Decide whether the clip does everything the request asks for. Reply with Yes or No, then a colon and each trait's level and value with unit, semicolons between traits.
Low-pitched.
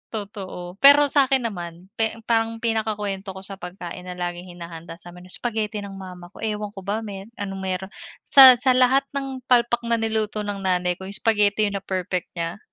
No: high, 205 Hz